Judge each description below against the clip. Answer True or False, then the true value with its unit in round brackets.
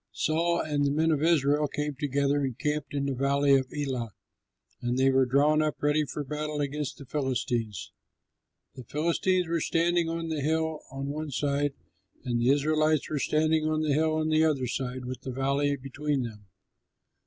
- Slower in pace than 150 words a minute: False (185 wpm)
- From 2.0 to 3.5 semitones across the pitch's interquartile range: True (2.5 semitones)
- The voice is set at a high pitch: False (145 Hz)